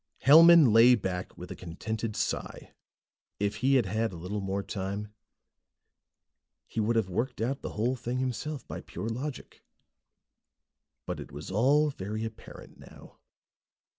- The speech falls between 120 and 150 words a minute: Yes, average, 145 wpm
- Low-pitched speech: Yes, low, 110 Hz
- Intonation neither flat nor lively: Yes, average, 4.4 semitones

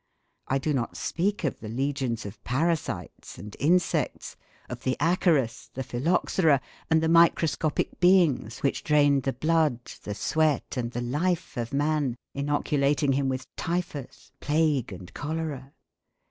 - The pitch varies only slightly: No, average, 3.9 semitones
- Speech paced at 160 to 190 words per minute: No, average, 140 wpm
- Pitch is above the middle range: No, medium, 145 Hz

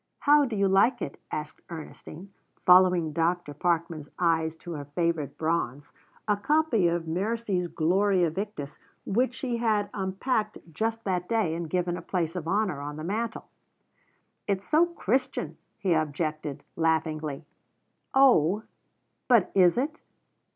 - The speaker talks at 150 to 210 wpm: No, slow, 135 wpm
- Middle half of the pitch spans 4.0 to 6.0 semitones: Yes, average, 5.0 semitones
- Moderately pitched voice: Yes, medium, 180 Hz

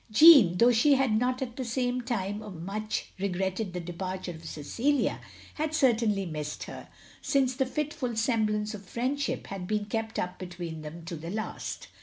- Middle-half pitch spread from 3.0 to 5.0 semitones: No, wide, 5.6 semitones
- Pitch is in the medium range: No, high, 215 Hz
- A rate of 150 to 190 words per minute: Yes, average, 165 wpm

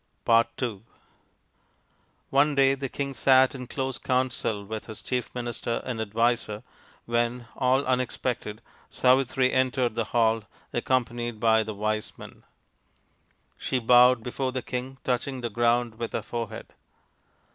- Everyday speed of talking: No, slow, 130 wpm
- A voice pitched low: Yes, low, 120 Hz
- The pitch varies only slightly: Yes, narrow, 2.1 semitones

